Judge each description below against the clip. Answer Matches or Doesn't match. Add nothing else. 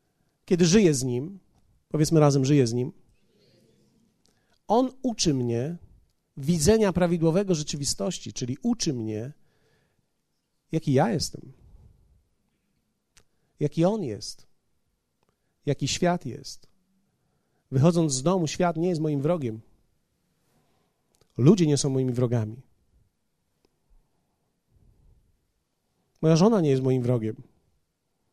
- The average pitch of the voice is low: Doesn't match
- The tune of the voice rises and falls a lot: Matches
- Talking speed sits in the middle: Doesn't match